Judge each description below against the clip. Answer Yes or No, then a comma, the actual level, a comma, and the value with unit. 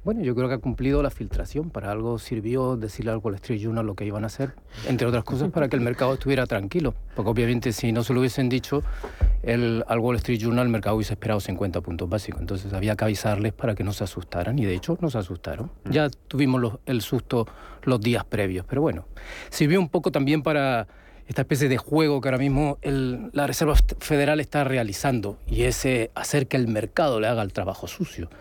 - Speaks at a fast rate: Yes, fast, 220 wpm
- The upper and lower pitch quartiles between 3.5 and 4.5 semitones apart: Yes, average, 4.2 semitones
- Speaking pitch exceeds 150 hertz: No, low, 120 Hz